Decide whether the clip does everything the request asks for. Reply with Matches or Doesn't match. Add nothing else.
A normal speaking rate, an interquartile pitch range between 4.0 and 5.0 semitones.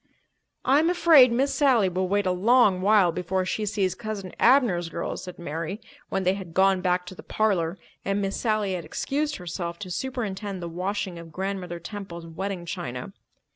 Doesn't match